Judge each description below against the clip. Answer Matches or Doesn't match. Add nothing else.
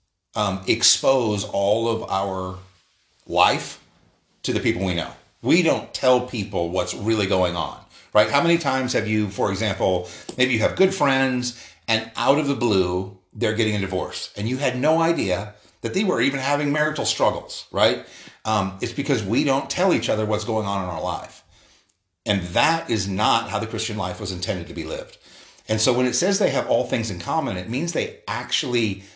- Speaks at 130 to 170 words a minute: Doesn't match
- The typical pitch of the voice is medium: Doesn't match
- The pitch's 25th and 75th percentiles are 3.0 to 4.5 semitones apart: Doesn't match